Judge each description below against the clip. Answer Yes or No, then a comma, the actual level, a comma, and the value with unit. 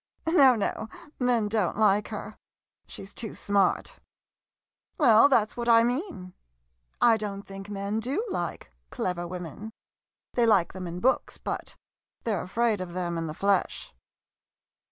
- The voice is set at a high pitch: Yes, high, 210 Hz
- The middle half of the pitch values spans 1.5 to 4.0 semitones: No, average, 4.4 semitones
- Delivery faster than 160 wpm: No, average, 155 wpm